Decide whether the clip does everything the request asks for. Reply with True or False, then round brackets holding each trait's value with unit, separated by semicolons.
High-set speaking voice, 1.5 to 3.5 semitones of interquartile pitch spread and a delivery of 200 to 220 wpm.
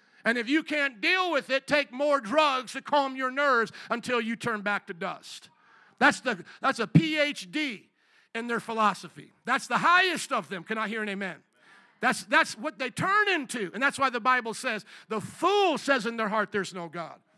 False (250 Hz; 4.9 semitones; 205 wpm)